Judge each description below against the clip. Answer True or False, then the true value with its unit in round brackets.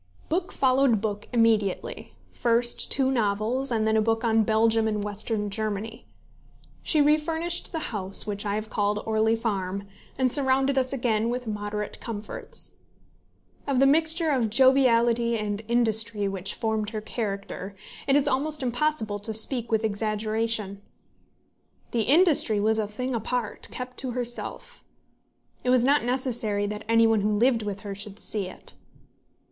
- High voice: True (225 Hz)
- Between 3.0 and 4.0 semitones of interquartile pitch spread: True (3.5 semitones)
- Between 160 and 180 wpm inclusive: False (150 wpm)